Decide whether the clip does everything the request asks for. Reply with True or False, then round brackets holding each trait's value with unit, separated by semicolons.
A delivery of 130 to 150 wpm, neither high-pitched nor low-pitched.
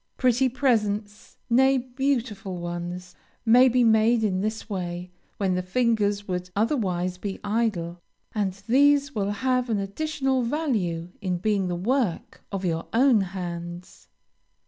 False (135 wpm; 210 Hz)